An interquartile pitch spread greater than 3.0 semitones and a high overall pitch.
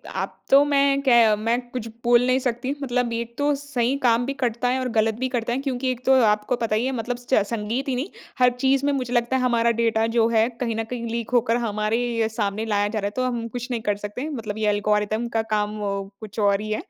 No: average, 2.7 semitones; high, 235 Hz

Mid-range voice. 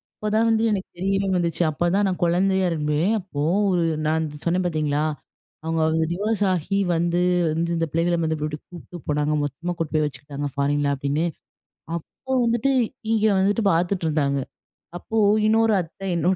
Yes: medium, 170 Hz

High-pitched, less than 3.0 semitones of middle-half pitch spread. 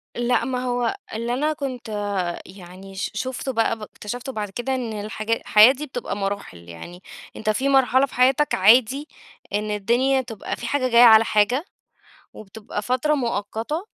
No: high, 235 Hz; average, 3.7 semitones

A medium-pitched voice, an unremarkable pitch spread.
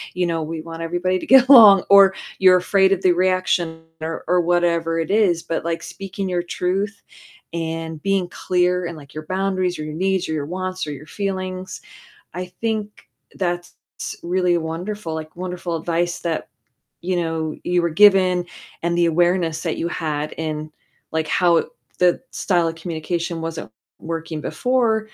No: medium, 175 Hz; narrow, 2.2 semitones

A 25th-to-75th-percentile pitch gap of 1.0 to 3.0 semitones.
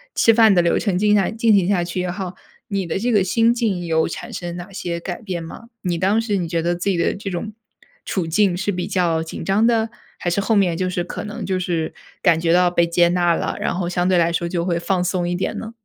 Yes: narrow, 2.6 semitones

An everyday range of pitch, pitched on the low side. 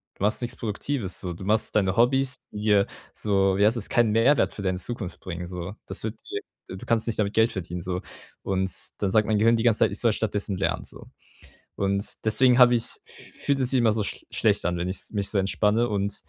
Yes: average, 3.2 semitones; low, 105 Hz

